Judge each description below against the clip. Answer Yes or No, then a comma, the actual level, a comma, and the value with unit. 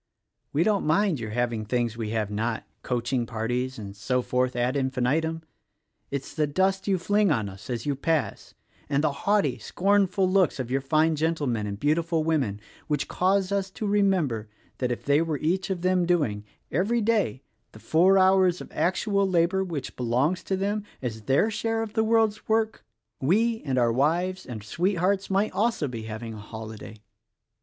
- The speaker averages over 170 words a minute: Yes, average, 185 wpm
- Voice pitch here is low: No, medium, 155 Hz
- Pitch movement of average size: No, wide, 7.8 semitones